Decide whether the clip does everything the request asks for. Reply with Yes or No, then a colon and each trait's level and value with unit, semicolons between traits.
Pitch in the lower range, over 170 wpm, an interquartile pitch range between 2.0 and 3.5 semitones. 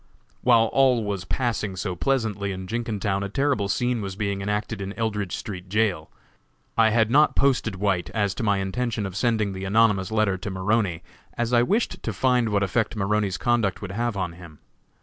Yes: low, 105 Hz; average, 190 wpm; average, 3.1 semitones